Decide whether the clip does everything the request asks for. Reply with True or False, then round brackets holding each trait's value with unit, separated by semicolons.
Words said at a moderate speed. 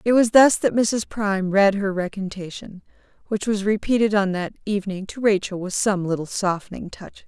True (180 wpm)